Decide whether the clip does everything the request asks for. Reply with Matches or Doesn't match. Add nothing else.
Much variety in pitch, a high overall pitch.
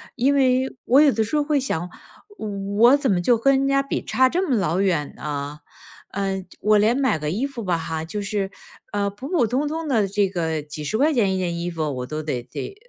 Matches